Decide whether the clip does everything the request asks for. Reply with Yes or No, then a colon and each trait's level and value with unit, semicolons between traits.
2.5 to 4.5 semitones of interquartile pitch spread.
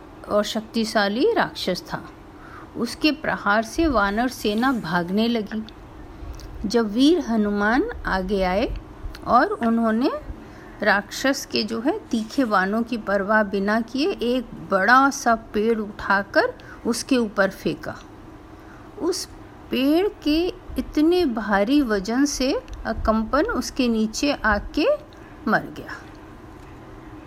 No: average, 5.2 semitones